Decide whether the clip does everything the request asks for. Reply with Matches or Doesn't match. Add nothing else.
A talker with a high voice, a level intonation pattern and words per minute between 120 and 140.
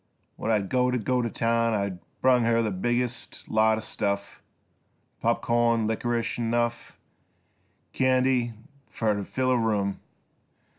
Doesn't match